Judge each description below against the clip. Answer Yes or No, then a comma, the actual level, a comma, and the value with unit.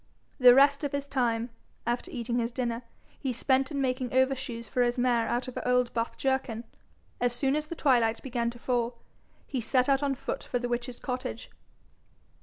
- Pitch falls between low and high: No, very high, 250 Hz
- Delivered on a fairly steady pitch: Yes, narrow, 2.1 semitones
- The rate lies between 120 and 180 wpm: No, average, 195 wpm